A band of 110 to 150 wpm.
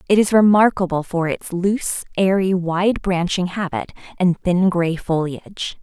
Yes: average, 145 wpm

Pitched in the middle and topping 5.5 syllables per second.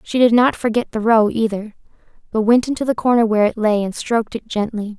No: high, 225 Hz; 6.0 syllables/s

